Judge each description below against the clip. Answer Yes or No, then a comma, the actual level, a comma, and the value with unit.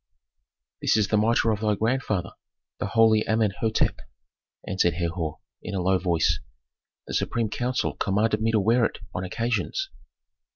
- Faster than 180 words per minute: No, average, 150 wpm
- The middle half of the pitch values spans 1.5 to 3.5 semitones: Yes, average, 3.1 semitones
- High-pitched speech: No, low, 110 Hz